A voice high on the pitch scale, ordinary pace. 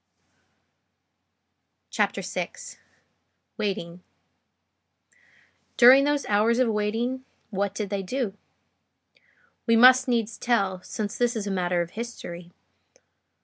No: high, 215 Hz; slow, 100 wpm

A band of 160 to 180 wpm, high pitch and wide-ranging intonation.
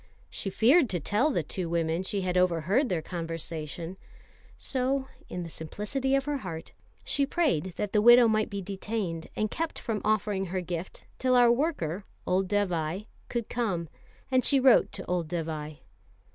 Yes: average, 170 wpm; high, 195 Hz; wide, 6.1 semitones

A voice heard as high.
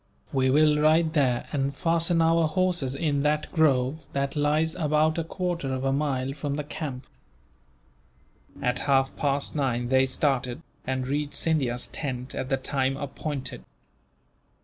No: medium, 140 Hz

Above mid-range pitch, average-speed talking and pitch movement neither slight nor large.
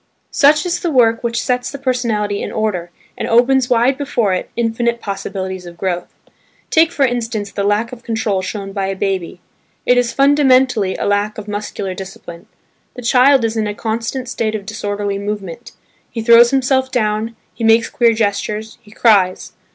Yes: high, 225 Hz; average, 175 wpm; average, 3.5 semitones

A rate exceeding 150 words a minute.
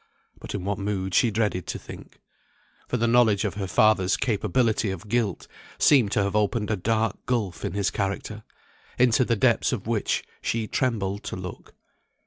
Yes: average, 175 wpm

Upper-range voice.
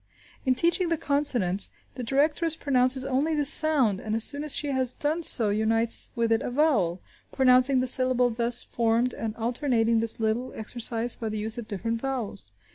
Yes: high, 245 Hz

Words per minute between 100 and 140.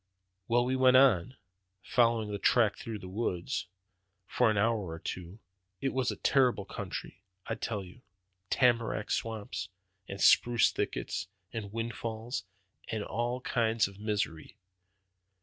Yes: slow, 135 wpm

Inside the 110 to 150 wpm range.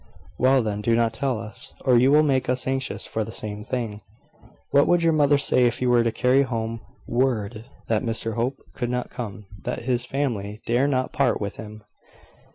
No: average, 200 wpm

